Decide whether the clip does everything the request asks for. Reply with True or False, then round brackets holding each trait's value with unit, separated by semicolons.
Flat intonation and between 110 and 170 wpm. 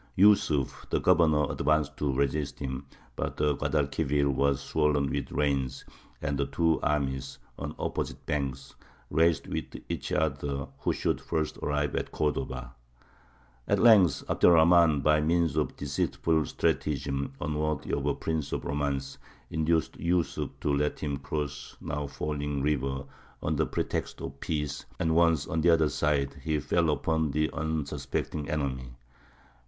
True (2.1 semitones; 150 wpm)